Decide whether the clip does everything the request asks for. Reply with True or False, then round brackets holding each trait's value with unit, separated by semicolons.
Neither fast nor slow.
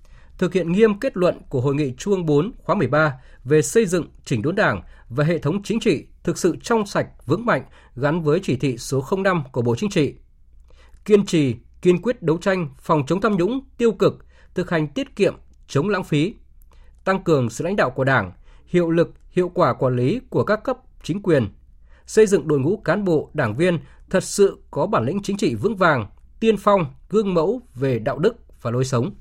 True (215 wpm)